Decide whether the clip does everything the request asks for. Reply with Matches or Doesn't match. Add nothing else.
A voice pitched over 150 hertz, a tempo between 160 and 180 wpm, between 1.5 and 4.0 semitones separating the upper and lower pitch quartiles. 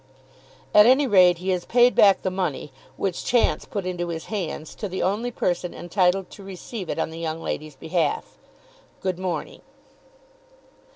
Matches